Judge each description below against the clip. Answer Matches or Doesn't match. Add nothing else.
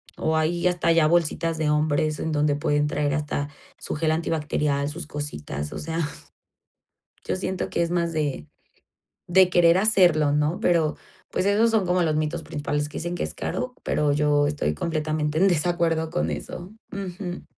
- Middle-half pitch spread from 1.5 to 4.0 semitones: Matches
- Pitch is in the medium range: Matches